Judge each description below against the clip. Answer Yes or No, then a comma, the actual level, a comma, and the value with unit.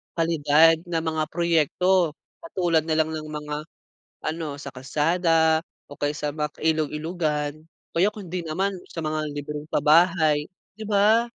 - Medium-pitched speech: Yes, medium, 160 Hz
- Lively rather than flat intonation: No, narrow, 2.4 semitones